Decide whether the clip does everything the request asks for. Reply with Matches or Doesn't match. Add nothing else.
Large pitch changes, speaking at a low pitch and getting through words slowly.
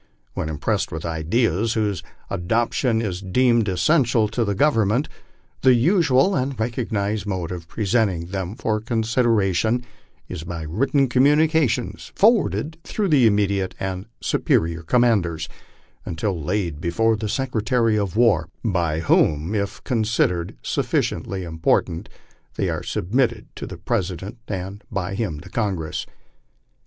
Doesn't match